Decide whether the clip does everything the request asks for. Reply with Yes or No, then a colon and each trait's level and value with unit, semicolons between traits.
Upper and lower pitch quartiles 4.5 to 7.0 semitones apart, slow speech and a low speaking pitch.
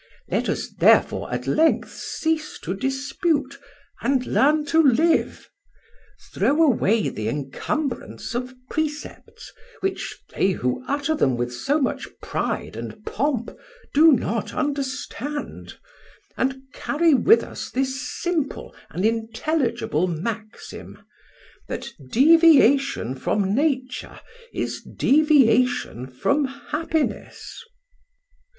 No: average, 5.3 semitones; slow, 105 wpm; very high, 270 Hz